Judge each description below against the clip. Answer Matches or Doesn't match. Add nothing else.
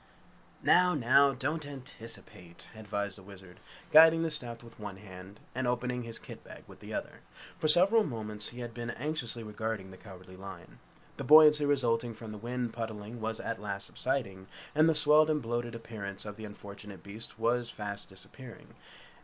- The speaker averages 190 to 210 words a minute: Doesn't match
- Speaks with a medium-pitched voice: Doesn't match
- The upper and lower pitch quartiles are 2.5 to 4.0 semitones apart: Doesn't match